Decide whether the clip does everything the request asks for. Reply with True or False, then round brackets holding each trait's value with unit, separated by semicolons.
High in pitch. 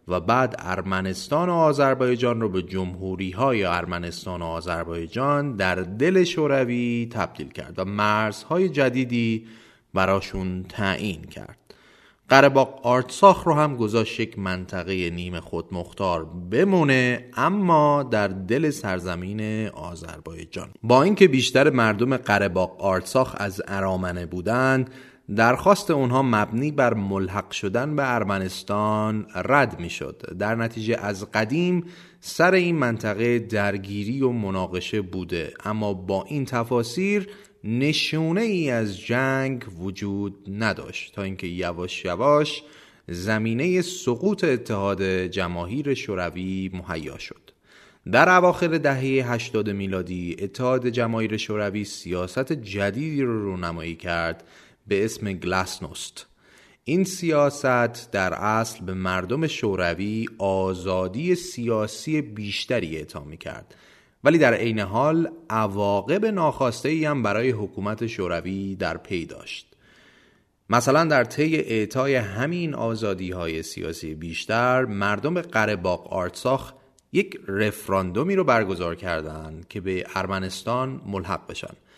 False (110 Hz)